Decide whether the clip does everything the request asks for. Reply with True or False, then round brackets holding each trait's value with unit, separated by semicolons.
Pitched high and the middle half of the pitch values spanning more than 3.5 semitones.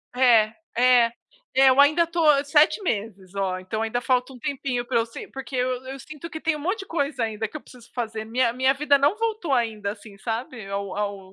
True (250 Hz; 4.4 semitones)